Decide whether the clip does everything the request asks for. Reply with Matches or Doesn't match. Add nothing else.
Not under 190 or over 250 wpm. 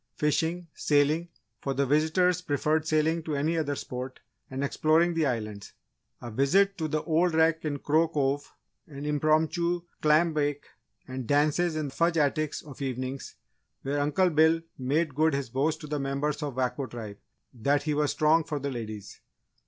Doesn't match